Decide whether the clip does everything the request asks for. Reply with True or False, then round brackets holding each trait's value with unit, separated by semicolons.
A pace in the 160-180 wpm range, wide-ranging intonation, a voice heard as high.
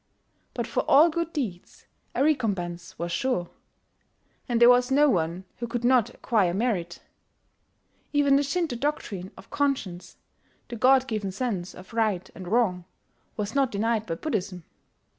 False (150 wpm; 6.3 semitones; 225 Hz)